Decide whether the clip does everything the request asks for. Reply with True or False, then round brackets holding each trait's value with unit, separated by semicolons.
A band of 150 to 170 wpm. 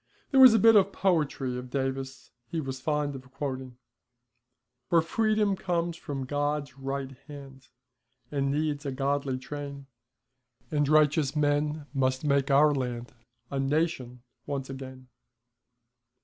False (135 wpm)